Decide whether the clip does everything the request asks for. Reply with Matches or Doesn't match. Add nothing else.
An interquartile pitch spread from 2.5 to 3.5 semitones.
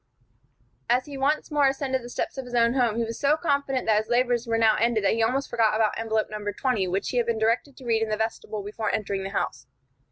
Matches